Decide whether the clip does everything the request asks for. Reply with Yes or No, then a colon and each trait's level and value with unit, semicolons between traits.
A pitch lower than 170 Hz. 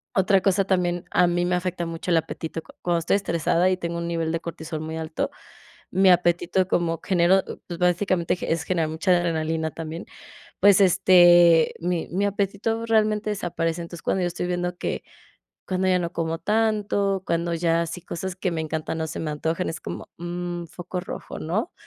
No: medium, 175 Hz